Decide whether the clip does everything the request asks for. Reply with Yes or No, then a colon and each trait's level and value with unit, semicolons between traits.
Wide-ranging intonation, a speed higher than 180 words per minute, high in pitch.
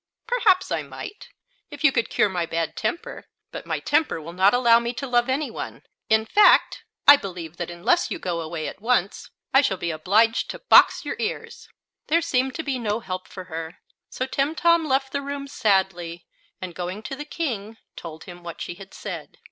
Yes: wide, 8.0 semitones; average, 200 wpm; high, 225 Hz